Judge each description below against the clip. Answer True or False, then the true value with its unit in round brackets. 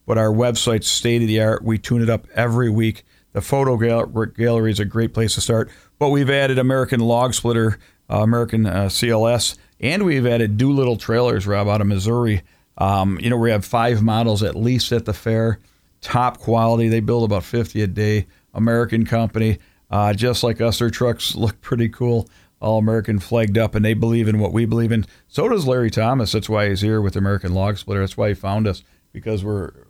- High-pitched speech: False (110 Hz)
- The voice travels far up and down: False (2.3 semitones)